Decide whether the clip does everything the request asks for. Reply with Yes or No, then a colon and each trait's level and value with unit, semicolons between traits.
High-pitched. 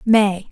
Yes: high, 205 Hz